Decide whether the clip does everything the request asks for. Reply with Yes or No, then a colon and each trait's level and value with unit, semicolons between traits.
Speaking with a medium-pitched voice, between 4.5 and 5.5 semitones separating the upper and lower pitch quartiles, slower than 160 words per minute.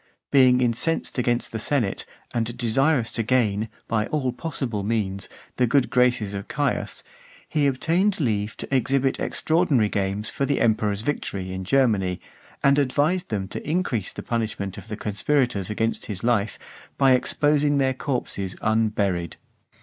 No: low, 120 Hz; average, 4.8 semitones; average, 150 wpm